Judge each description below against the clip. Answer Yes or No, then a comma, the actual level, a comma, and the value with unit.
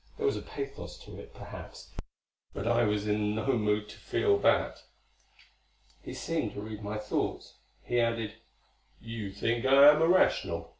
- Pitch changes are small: No, average, 4.7 semitones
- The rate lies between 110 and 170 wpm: Yes, average, 160 wpm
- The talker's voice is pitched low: Yes, low, 115 Hz